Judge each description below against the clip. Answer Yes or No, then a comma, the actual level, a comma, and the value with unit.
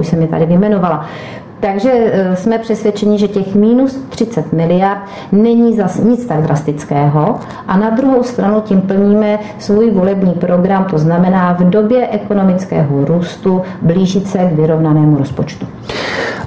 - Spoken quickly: No, average, 140 wpm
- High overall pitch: Yes, high, 195 Hz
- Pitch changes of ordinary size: Yes, average, 3.9 semitones